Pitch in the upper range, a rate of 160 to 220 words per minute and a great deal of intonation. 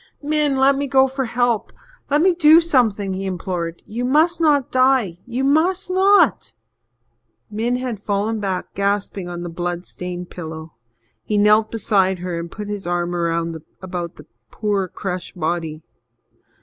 No: high, 205 Hz; average, 150 wpm; wide, 7.0 semitones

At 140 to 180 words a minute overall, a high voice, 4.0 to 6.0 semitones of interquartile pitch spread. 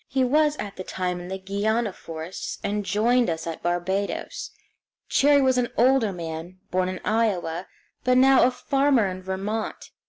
Yes: average, 165 wpm; high, 205 Hz; wide, 5.4 semitones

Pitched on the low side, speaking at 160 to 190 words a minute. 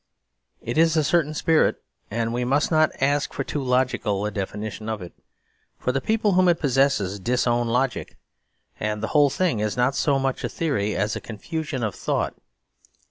Yes: low, 130 Hz; average, 185 wpm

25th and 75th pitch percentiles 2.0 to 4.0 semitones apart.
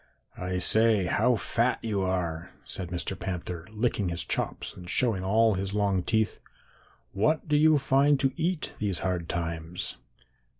No: average, 4.7 semitones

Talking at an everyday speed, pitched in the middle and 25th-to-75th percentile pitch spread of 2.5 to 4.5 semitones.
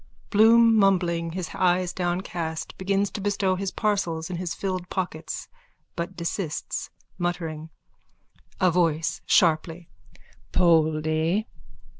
No: slow, 105 wpm; medium, 175 Hz; average, 2.8 semitones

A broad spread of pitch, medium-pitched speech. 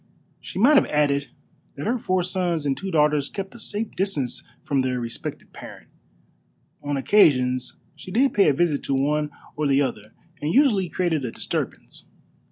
Yes: wide, 5.7 semitones; medium, 150 Hz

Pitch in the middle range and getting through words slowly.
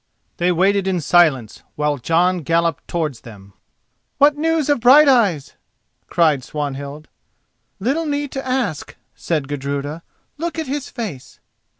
Yes: medium, 175 Hz; slow, 125 wpm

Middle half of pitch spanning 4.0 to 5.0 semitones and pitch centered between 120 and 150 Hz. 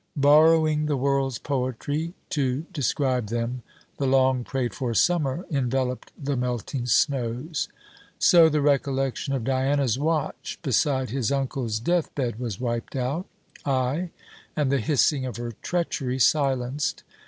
No: average, 2.7 semitones; low, 135 Hz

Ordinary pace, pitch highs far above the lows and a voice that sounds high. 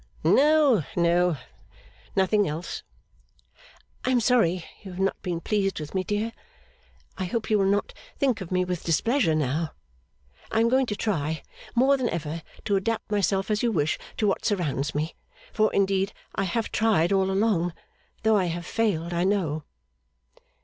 No: average, 165 wpm; average, 4.3 semitones; high, 195 Hz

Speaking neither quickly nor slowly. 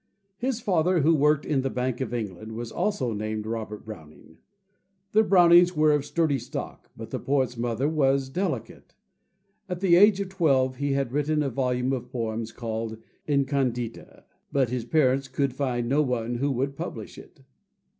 Yes: average, 170 wpm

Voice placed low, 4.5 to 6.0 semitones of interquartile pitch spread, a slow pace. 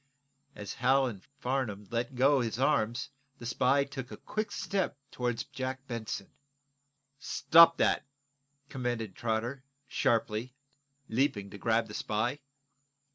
No: low, 125 Hz; average, 3.2 semitones; slow, 125 wpm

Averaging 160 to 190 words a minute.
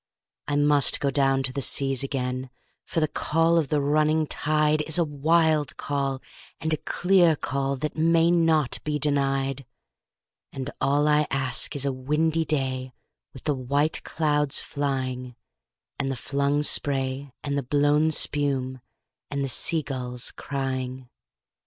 No: average, 150 wpm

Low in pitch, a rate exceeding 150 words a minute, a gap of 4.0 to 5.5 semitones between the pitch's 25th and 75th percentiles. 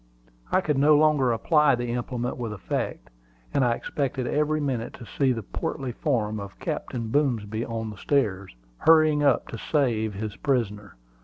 Yes: low, 125 Hz; average, 165 wpm; average, 4.8 semitones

